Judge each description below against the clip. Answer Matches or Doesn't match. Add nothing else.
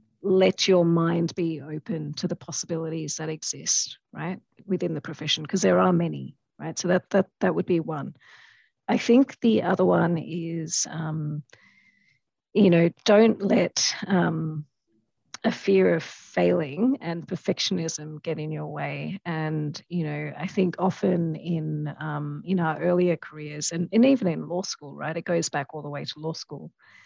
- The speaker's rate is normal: Matches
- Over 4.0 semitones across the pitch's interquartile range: Doesn't match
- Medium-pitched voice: Matches